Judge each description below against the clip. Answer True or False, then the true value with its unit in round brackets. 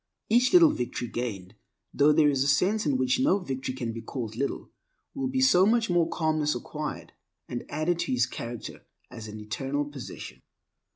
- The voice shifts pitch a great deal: True (6.6 semitones)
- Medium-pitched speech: True (145 Hz)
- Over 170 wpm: True (180 wpm)